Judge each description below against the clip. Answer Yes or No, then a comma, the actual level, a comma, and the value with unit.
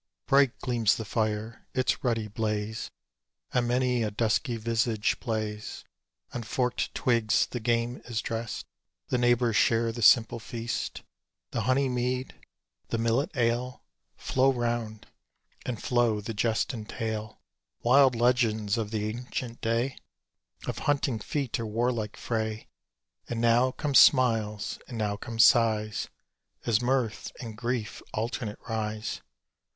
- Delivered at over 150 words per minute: No, slow, 135 wpm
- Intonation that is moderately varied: No, narrow, 2.1 semitones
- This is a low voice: Yes, low, 115 Hz